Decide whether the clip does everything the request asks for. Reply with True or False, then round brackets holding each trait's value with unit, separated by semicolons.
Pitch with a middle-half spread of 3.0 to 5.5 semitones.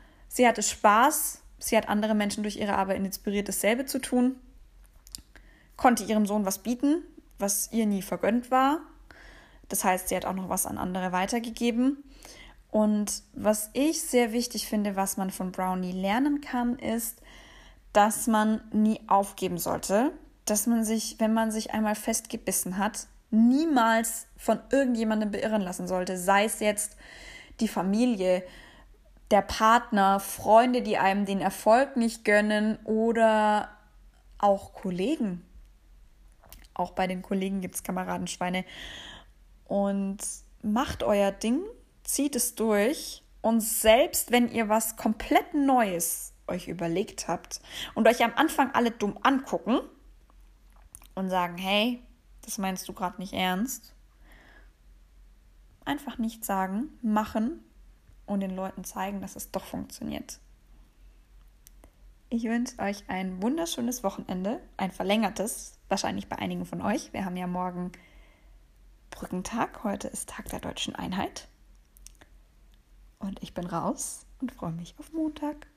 True (3.8 semitones)